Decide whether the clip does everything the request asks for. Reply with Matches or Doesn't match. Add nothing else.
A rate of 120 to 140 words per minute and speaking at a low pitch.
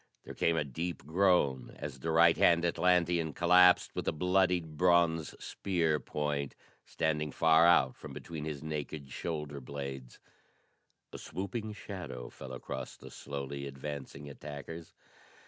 Matches